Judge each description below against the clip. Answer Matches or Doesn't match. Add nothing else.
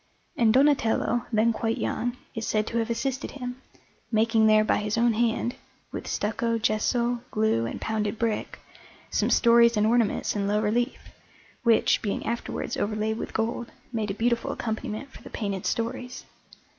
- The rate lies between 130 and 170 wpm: Matches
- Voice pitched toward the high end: Matches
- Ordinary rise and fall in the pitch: Doesn't match